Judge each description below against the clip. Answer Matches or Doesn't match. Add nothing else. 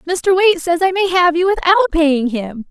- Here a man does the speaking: Doesn't match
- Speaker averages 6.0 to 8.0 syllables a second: Doesn't match